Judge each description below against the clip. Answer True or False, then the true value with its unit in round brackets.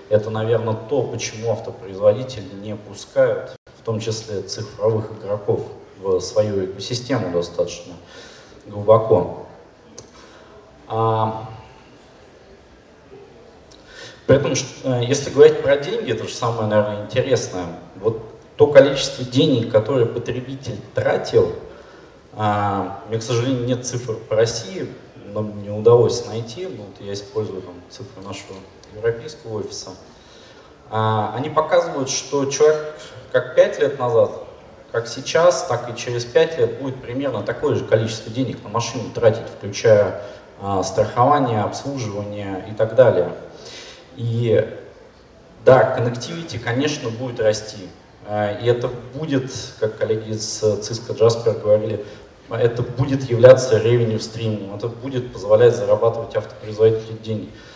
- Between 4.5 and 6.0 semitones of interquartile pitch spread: True (5.3 semitones)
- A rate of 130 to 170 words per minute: False (115 wpm)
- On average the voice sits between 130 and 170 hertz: False (120 Hz)